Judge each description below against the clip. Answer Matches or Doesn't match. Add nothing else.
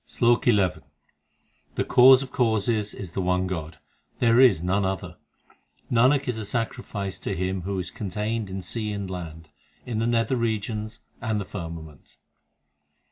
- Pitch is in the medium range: Doesn't match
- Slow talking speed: Doesn't match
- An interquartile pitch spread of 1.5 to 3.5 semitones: Doesn't match